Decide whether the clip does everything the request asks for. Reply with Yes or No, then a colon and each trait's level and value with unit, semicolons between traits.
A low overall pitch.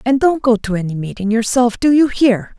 No: high, 235 Hz